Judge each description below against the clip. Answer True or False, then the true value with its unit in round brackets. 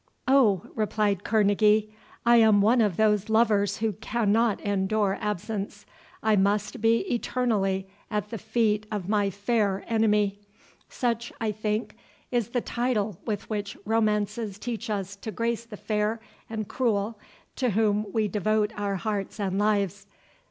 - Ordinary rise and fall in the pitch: False (1.8 semitones)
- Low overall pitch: False (210 Hz)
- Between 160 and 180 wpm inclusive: False (140 wpm)